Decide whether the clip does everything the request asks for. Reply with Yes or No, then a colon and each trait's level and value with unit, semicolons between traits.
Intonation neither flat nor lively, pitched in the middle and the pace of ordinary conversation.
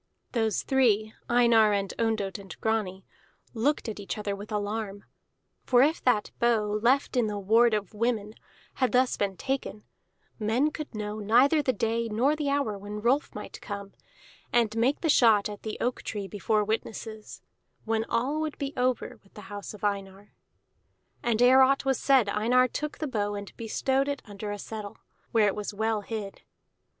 No: average, 3.3 semitones; high, 220 Hz; average, 180 wpm